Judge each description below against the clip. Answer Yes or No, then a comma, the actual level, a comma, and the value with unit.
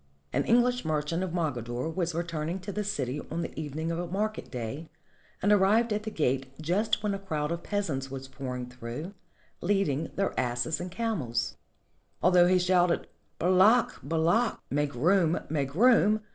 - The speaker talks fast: No, average, 175 wpm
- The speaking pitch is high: No, medium, 170 Hz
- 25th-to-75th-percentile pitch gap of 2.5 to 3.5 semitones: No, wide, 5.5 semitones